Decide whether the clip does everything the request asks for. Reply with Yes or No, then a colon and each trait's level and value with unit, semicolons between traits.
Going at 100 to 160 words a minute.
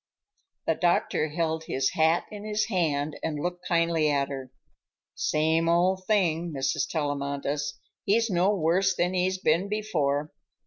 Yes: average, 140 wpm